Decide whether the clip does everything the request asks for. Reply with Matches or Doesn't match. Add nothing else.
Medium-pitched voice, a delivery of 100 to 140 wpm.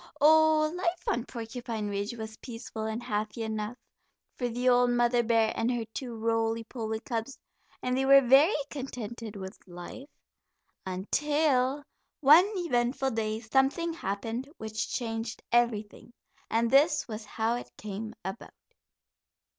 Doesn't match